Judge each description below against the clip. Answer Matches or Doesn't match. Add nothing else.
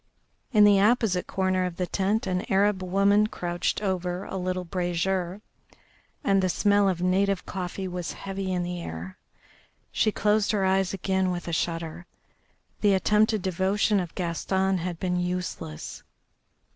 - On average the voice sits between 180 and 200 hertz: Matches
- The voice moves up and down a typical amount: Doesn't match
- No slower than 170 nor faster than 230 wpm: Doesn't match